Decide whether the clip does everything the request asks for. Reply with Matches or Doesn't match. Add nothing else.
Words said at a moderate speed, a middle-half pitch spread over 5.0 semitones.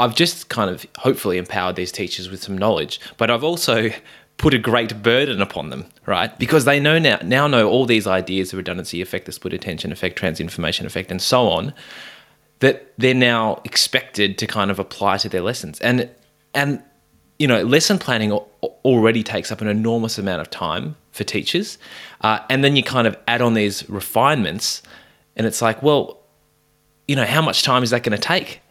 Doesn't match